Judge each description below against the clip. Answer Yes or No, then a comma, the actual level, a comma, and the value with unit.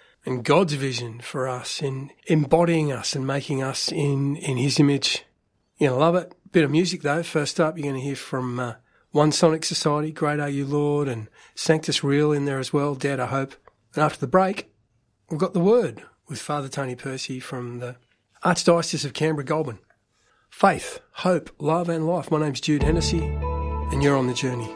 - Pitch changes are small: No, average, 3.6 semitones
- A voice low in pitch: No, medium, 145 Hz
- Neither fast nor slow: Yes, average, 195 wpm